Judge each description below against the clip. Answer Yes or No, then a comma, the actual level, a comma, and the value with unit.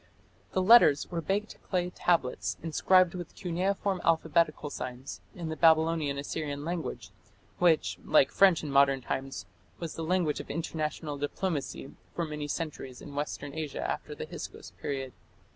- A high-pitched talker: No, medium, 160 Hz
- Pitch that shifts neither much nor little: Yes, average, 3.5 semitones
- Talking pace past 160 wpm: No, average, 145 wpm